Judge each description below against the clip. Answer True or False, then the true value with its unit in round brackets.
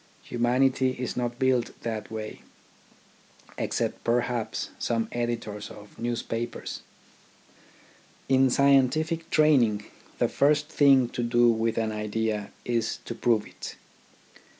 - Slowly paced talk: True (115 wpm)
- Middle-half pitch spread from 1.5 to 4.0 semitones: True (2.7 semitones)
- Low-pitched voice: True (120 Hz)